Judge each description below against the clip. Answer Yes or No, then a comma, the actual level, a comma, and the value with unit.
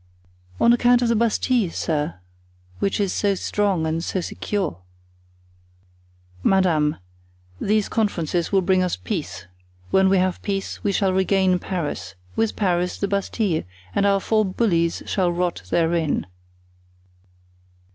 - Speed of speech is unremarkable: No, slow, 130 wpm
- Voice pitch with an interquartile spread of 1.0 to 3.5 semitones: Yes, average, 3.0 semitones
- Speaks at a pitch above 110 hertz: Yes, high, 190 Hz